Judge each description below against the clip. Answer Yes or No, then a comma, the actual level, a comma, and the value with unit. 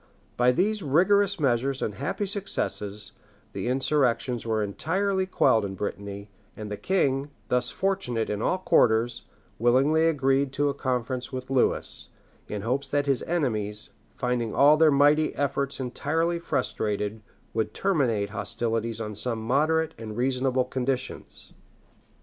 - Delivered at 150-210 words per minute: No, slow, 135 wpm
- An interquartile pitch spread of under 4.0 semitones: No, average, 5.1 semitones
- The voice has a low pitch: Yes, low, 130 Hz